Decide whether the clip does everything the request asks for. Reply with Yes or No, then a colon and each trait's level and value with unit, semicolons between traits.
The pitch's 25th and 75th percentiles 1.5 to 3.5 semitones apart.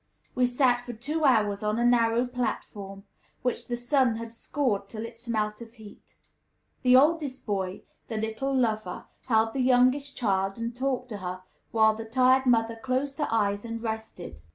Yes: average, 2.7 semitones